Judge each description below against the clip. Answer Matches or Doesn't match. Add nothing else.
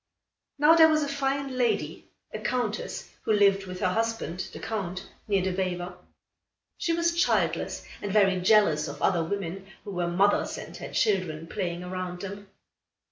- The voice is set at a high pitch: Matches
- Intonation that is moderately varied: Matches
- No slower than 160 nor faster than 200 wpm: Matches